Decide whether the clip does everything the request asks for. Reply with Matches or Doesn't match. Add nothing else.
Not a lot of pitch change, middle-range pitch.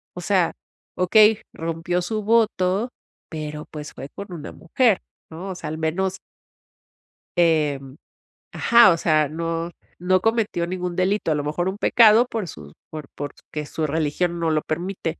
Doesn't match